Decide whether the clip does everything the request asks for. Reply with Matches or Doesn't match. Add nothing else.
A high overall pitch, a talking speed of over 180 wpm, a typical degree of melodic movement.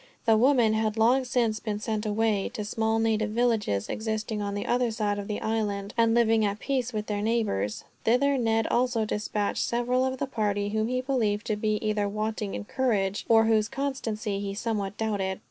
Doesn't match